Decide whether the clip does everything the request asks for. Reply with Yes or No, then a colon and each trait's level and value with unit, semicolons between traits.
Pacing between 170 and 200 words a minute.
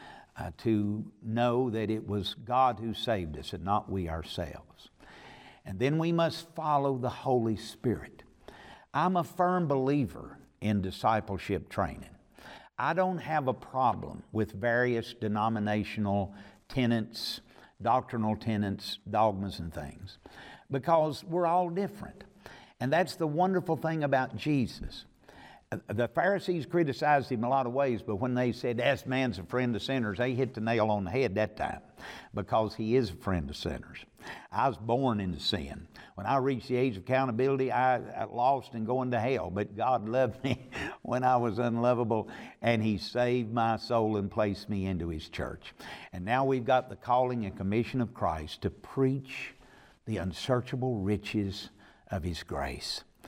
No: average, 160 wpm